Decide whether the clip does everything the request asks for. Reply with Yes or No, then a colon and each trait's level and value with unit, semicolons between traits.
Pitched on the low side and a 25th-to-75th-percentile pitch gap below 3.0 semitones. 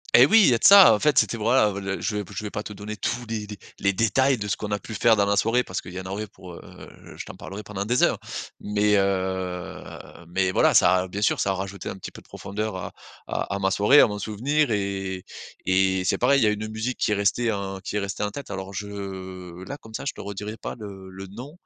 Yes: low, 100 Hz; narrow, 2.5 semitones